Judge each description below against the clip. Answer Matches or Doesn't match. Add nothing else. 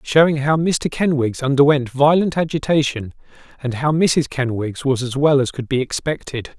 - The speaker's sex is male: Matches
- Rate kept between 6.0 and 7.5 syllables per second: Doesn't match